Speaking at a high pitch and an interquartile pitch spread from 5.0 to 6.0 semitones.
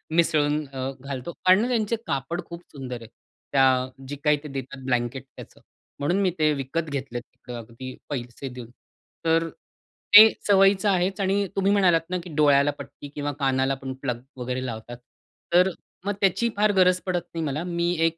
No: medium, 145 Hz; wide, 5.5 semitones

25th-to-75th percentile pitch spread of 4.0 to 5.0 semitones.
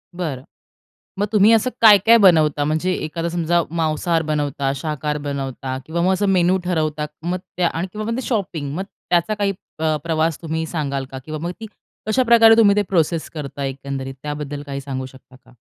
Yes: average, 4.5 semitones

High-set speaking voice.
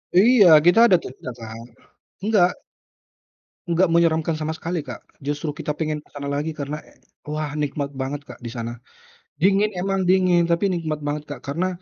No: medium, 155 Hz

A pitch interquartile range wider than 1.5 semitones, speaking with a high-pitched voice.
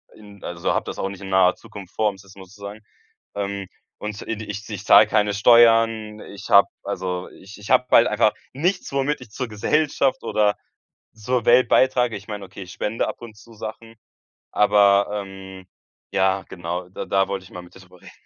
No: average, 2.8 semitones; low, 105 Hz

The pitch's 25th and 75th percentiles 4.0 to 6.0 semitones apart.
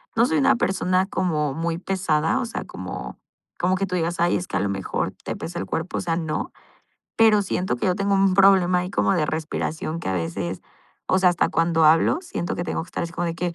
No: narrow, 2.6 semitones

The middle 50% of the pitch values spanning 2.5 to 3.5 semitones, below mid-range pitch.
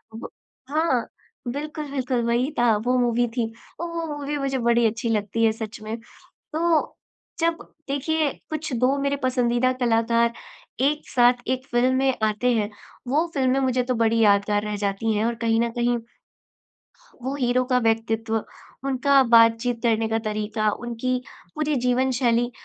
No: average, 2.8 semitones; high, 245 Hz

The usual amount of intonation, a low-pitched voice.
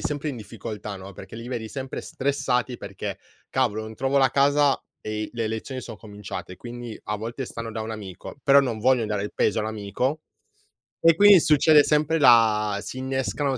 Yes: average, 4.1 semitones; low, 120 Hz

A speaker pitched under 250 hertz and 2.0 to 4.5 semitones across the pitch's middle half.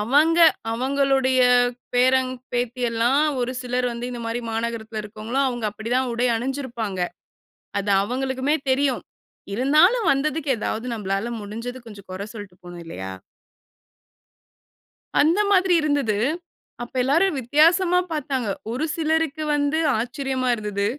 No: very high, 255 Hz; average, 4.1 semitones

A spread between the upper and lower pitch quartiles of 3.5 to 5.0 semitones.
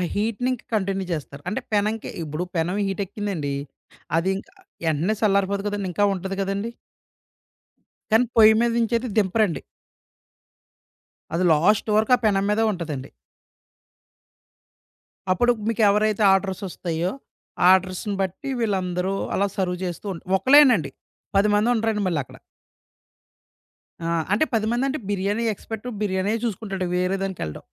No: average, 3.0 semitones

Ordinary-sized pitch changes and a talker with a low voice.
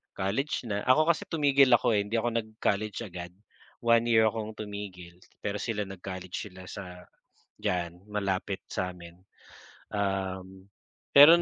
Yes: average, 3.3 semitones; low, 100 Hz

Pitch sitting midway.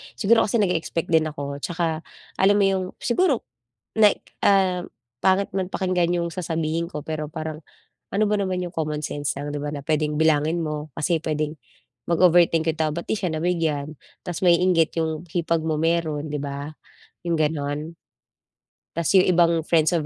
Yes: medium, 165 Hz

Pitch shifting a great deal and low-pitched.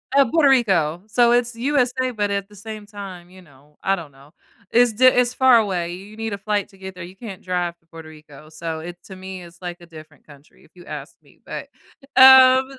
No: wide, 5.7 semitones; high, 195 Hz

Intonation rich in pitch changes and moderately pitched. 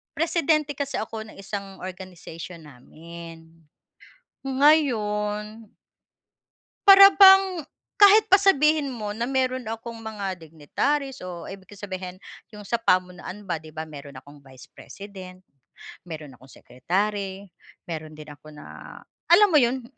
No: wide, 8.1 semitones; high, 205 Hz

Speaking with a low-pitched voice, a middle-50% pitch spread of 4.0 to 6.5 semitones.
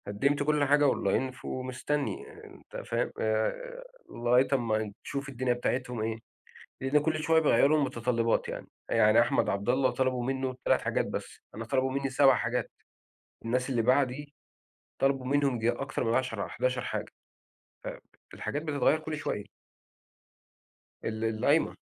No: low, 130 Hz; average, 3.1 semitones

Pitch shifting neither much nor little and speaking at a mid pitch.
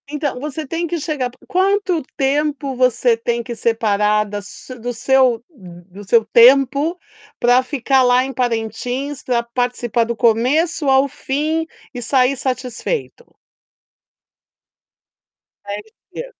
No: average, 3.7 semitones; very high, 255 Hz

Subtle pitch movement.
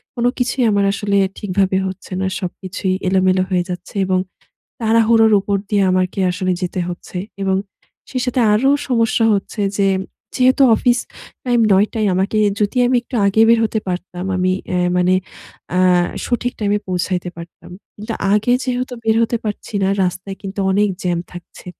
No: average, 3.5 semitones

